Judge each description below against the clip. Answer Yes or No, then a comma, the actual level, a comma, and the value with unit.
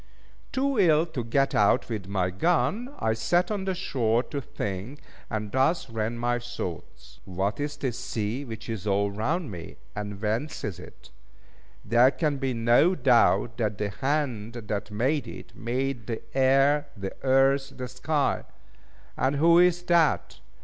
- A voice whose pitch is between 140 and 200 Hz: No, low, 125 Hz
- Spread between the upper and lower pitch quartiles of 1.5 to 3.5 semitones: No, average, 5.3 semitones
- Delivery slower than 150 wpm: No, average, 160 wpm